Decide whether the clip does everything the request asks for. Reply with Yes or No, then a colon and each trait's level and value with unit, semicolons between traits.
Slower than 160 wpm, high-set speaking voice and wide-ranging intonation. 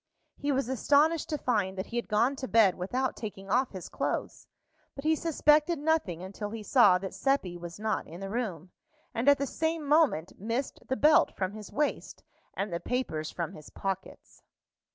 No: average, 190 wpm; high, 230 Hz; wide, 6.9 semitones